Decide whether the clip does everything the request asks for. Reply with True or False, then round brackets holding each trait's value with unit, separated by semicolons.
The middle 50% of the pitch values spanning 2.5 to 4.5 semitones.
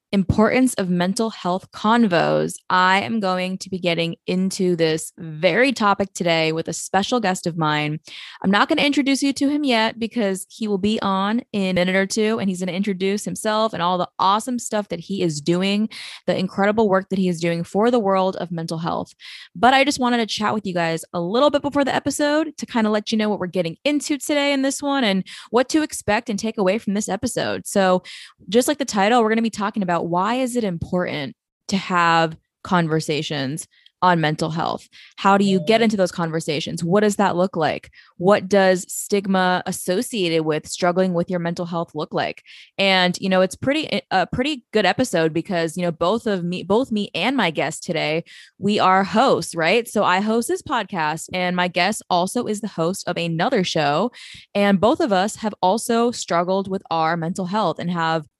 True (4.2 semitones)